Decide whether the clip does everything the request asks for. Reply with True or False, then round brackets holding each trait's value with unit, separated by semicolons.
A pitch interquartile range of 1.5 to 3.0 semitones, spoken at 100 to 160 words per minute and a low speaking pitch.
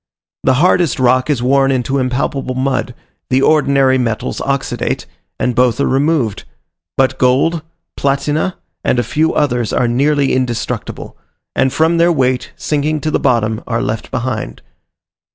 True (2.6 semitones; 145 wpm; 130 Hz)